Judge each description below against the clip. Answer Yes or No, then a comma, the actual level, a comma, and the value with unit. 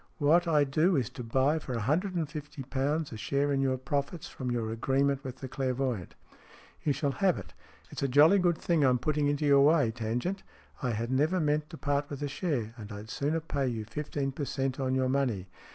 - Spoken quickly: Yes, fast, 220 wpm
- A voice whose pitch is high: No, medium, 140 Hz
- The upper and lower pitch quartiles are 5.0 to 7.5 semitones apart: No, average, 2.9 semitones